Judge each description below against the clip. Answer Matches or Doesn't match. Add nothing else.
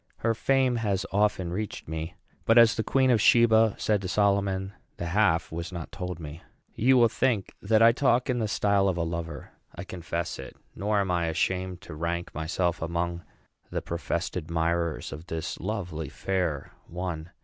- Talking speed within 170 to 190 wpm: Matches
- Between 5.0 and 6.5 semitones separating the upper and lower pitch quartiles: Doesn't match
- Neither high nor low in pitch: Doesn't match